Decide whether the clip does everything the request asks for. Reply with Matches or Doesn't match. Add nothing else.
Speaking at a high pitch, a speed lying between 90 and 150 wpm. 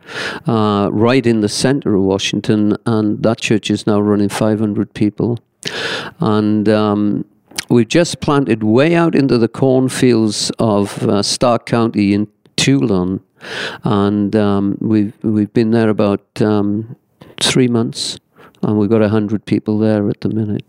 Doesn't match